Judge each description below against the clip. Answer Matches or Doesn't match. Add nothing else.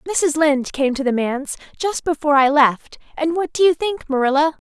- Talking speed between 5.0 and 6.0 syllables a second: Matches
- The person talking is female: Matches